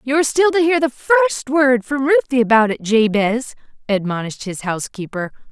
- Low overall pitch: No, very high, 250 Hz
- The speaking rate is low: No, average, 175 wpm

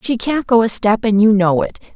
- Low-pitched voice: No, high, 220 Hz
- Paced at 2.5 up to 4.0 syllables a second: No, 5.4 syllables/s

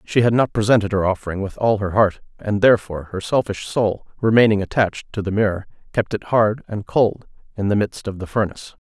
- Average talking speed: No, fast, 210 wpm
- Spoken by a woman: No, male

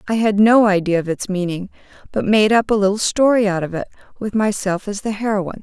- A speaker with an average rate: No, fast, 225 wpm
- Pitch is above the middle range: Yes, high, 205 Hz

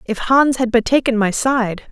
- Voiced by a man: No, female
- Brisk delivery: Yes, fast, 220 wpm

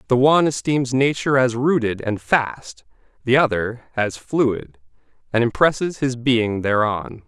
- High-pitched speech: No, low, 120 Hz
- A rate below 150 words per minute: Yes, average, 140 wpm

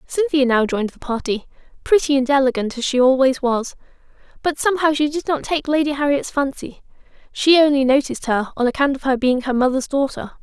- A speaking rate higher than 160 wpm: Yes, average, 190 wpm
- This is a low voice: No, very high, 275 Hz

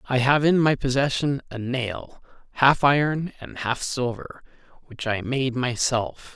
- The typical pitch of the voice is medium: No, low, 130 Hz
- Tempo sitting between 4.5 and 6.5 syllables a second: No, 4.0 syllables/s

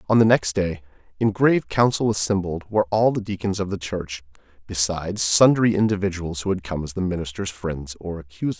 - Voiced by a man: Yes, male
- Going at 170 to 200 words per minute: Yes, average, 190 wpm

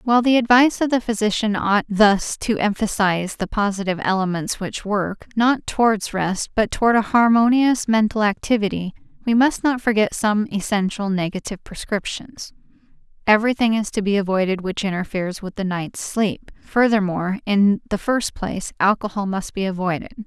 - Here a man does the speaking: No, female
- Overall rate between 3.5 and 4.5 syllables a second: No, 5.2 syllables/s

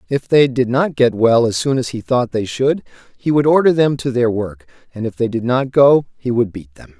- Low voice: Yes, low, 125 Hz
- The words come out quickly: Yes, fast, 255 wpm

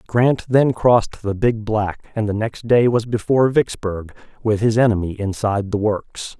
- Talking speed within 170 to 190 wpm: Yes, average, 180 wpm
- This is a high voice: No, low, 110 Hz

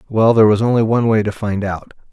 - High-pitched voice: No, low, 110 Hz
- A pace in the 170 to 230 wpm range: No, fast, 255 wpm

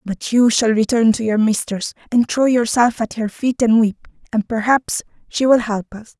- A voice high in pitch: Yes, high, 225 Hz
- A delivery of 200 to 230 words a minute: Yes, fast, 205 wpm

